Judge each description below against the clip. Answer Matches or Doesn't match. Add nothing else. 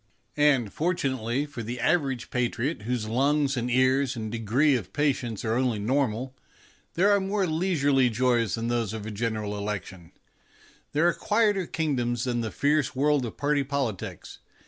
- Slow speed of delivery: Doesn't match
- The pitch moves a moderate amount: Matches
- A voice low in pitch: Matches